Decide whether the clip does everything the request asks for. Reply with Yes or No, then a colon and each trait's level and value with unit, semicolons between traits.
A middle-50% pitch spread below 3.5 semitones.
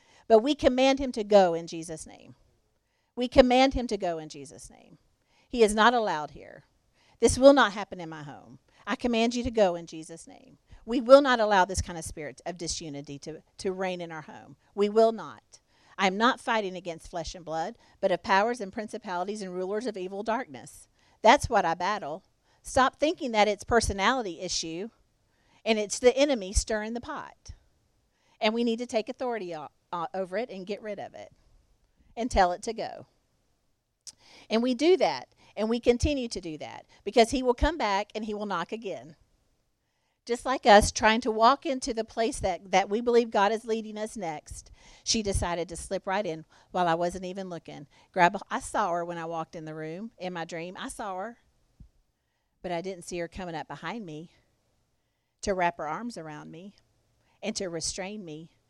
No: average, 5.2 semitones